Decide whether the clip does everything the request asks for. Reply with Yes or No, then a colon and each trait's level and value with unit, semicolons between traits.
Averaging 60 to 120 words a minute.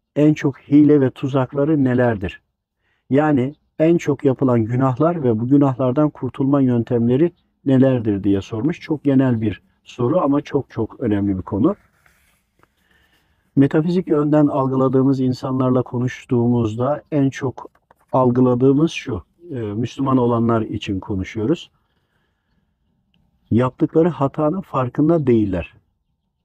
Yes: average, 105 wpm